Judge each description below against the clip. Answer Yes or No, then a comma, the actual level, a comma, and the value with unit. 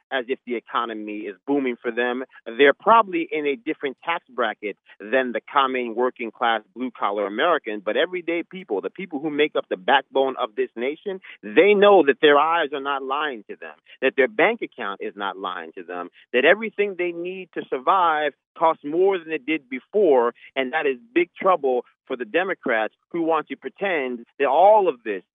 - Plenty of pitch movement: Yes, wide, 6.7 semitones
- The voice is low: No, medium, 150 Hz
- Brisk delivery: No, average, 195 wpm